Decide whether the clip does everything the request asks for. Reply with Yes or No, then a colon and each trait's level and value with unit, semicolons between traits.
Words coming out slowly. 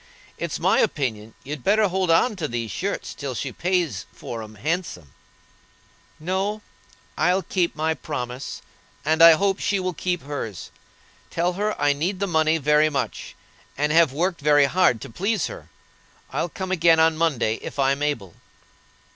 No: average, 165 wpm